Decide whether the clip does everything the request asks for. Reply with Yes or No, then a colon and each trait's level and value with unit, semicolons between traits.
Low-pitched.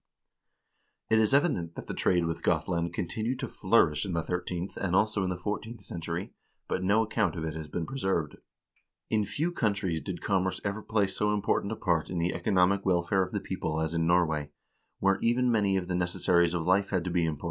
Yes: very low, 90 Hz